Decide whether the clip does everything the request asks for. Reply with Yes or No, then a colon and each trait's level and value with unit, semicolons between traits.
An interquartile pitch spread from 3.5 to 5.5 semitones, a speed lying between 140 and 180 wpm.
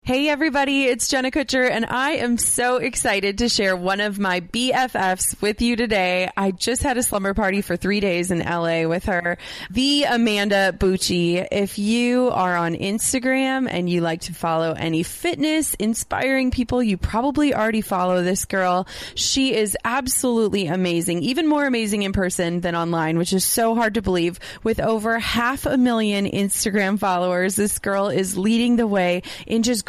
Yes: average, 5.1 semitones; average, 175 wpm